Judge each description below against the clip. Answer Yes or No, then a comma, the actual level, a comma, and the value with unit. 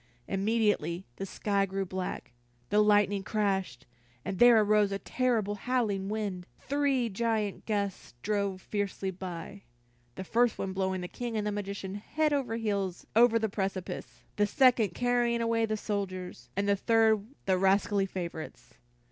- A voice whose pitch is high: Yes, high, 205 Hz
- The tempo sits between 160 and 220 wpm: No, average, 150 wpm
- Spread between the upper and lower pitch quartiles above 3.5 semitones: No, average, 2.7 semitones